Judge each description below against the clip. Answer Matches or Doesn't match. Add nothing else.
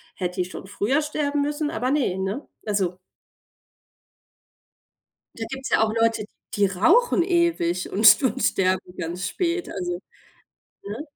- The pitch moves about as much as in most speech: Doesn't match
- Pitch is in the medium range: Doesn't match